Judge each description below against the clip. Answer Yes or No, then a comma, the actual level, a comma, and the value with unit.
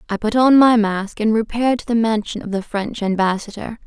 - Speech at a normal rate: No, fast, 215 wpm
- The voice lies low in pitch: No, high, 220 Hz